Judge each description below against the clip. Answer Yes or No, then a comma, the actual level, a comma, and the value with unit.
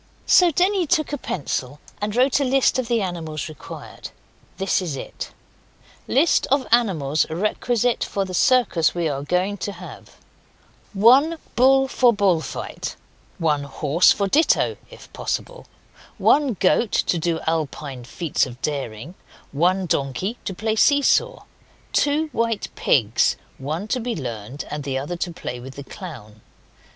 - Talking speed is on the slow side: No, average, 150 wpm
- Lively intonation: Yes, wide, 8.9 semitones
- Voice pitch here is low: No, medium, 185 Hz